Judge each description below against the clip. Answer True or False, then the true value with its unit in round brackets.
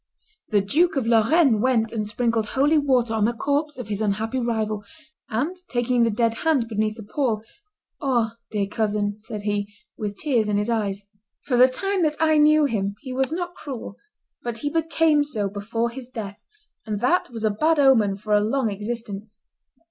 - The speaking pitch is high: True (230 Hz)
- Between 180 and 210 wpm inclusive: True (185 wpm)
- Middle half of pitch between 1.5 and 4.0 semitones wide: False (4.5 semitones)